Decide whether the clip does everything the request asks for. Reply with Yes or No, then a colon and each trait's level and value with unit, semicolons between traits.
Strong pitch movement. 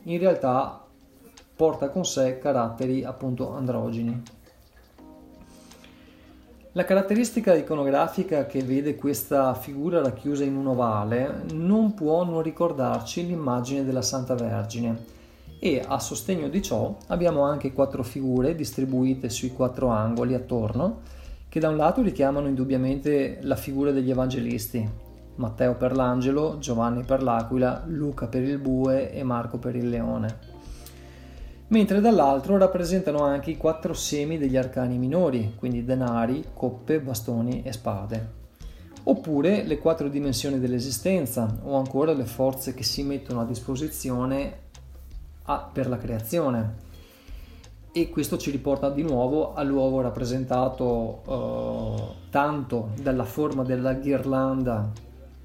No: average, 3.3 semitones